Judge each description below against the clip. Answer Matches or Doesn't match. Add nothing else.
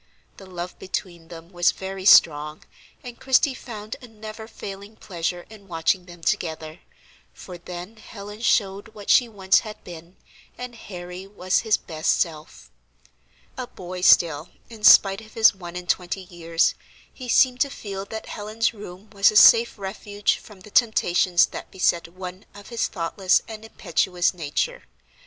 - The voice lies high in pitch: Matches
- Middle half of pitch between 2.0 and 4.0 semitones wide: Matches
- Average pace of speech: Matches